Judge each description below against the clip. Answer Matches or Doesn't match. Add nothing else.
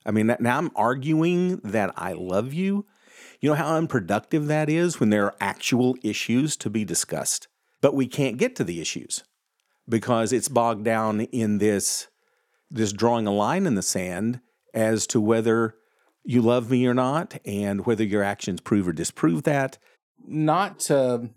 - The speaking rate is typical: Matches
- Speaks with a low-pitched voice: Matches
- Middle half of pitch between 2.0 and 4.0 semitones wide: Doesn't match